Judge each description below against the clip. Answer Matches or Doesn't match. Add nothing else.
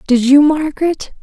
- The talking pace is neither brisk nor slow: Matches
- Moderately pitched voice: Doesn't match